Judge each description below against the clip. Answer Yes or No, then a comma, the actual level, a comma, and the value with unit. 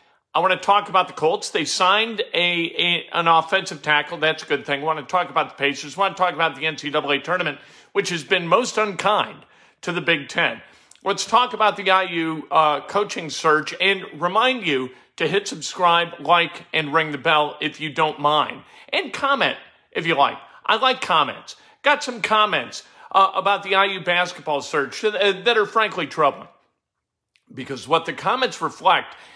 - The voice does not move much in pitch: No, average, 4.5 semitones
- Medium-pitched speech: Yes, medium, 175 Hz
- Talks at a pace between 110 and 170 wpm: No, average, 185 wpm